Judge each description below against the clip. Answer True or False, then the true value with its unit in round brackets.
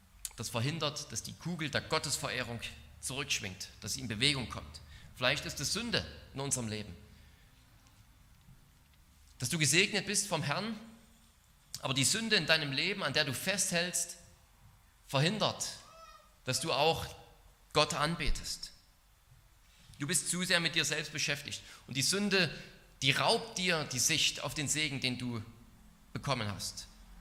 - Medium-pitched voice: True (145 Hz)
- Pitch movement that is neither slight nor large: False (6.7 semitones)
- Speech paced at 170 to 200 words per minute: False (145 wpm)